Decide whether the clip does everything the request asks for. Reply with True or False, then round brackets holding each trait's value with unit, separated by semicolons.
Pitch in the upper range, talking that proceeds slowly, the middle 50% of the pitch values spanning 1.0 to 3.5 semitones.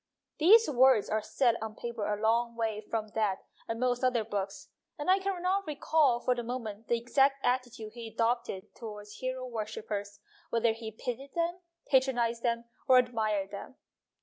False (235 Hz; 170 wpm; 2.9 semitones)